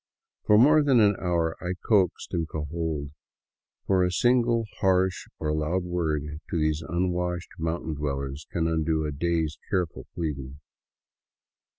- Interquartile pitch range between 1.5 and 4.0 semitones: Yes, average, 3.2 semitones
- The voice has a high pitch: No, very low, 85 Hz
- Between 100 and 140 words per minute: Yes, slow, 135 wpm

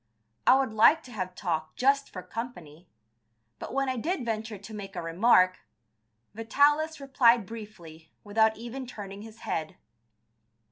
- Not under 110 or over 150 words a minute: Yes, average, 145 wpm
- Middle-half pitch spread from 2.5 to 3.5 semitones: No, average, 5.2 semitones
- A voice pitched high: Yes, high, 220 Hz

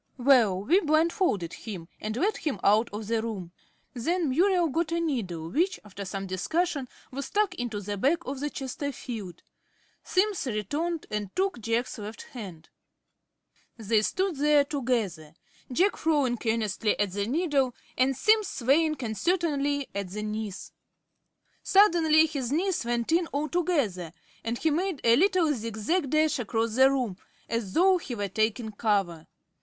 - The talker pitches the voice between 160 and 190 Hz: No, very high, 255 Hz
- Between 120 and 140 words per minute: No, average, 150 wpm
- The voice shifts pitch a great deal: Yes, wide, 7.2 semitones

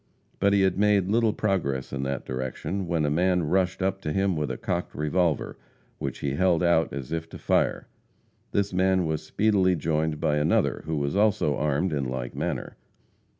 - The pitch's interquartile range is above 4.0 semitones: Yes, average, 4.4 semitones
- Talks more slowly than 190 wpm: No, average, 195 wpm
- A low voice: Yes, very low, 85 Hz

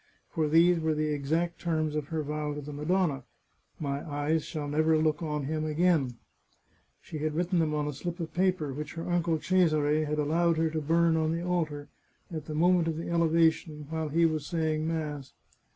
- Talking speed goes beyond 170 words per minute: Yes, average, 200 wpm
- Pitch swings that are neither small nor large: No, narrow, 1.9 semitones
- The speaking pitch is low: No, medium, 155 Hz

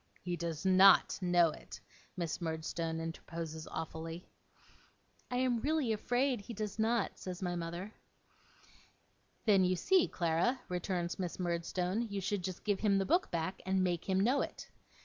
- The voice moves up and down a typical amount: Yes, average, 3.9 semitones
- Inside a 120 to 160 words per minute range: Yes, average, 155 wpm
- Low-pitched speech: No, medium, 185 Hz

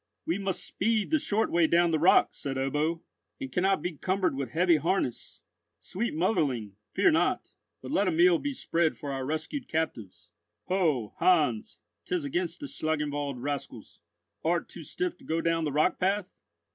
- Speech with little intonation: No, average, 4.3 semitones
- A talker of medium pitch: Yes, medium, 165 Hz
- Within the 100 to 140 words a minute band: No, average, 170 wpm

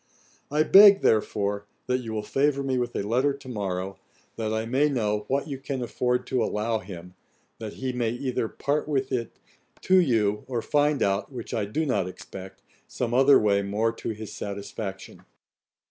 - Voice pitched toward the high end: No, low, 115 Hz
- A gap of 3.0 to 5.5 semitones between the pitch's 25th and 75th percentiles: Yes, average, 4.5 semitones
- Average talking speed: Yes, average, 180 wpm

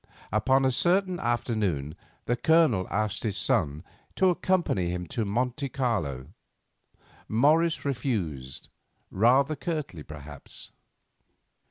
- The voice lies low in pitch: Yes, low, 115 Hz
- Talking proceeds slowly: Yes, slow, 100 wpm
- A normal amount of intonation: No, wide, 7.9 semitones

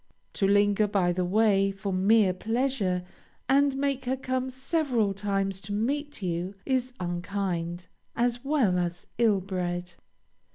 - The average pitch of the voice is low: No, high, 205 Hz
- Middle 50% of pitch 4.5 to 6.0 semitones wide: Yes, wide, 5.5 semitones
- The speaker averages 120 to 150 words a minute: Yes, slow, 135 wpm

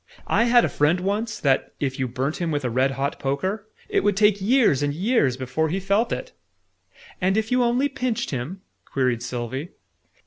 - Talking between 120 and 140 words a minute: No, average, 195 wpm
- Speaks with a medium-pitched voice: Yes, medium, 175 Hz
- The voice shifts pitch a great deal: Yes, wide, 8.3 semitones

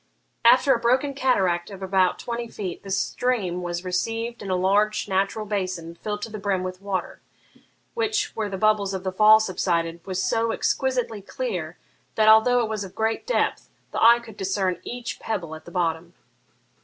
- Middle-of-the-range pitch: No, high, 205 Hz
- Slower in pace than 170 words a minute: No, average, 180 wpm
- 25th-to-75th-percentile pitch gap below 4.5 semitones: Yes, average, 3.8 semitones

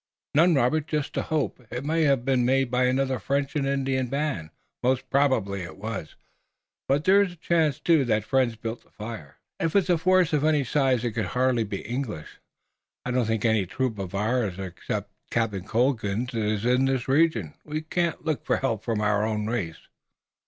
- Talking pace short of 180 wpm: No, average, 195 wpm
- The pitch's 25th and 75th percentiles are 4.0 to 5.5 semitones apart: Yes, average, 4.6 semitones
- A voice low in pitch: Yes, low, 125 Hz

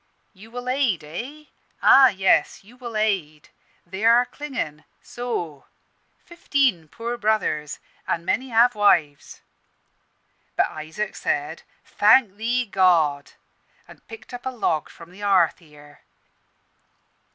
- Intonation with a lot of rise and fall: Yes, wide, 7.0 semitones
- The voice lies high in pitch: Yes, high, 205 Hz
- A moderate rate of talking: No, slow, 120 wpm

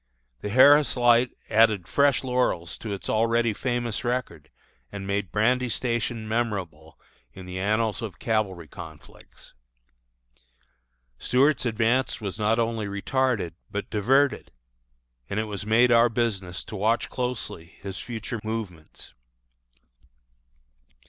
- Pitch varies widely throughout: No, average, 3.4 semitones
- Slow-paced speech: Yes, slow, 120 wpm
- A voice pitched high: No, low, 110 Hz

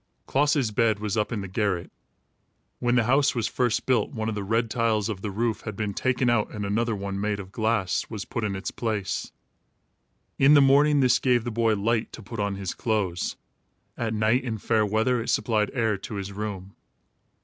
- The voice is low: Yes, low, 110 Hz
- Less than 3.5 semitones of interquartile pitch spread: Yes, narrow, 2.6 semitones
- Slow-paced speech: No, fast, 205 wpm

